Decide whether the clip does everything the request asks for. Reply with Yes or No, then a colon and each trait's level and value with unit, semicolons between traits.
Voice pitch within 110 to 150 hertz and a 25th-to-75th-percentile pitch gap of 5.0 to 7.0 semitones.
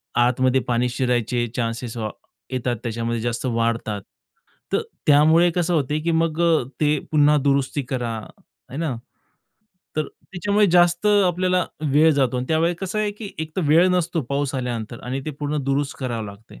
Yes: medium, 140 Hz; wide, 5.4 semitones